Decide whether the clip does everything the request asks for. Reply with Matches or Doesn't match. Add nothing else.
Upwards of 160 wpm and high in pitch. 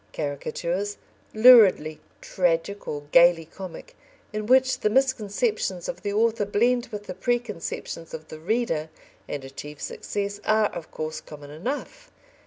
Doesn't match